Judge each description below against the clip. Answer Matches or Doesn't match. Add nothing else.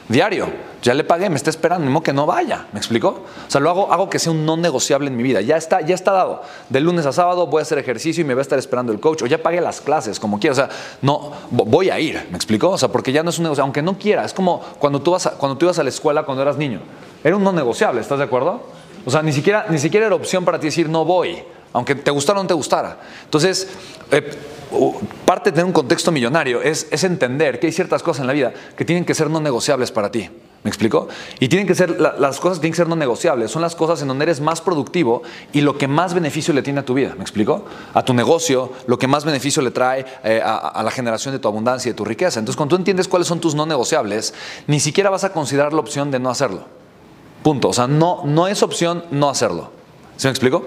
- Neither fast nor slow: Doesn't match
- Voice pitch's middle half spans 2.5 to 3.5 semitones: Doesn't match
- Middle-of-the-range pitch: Matches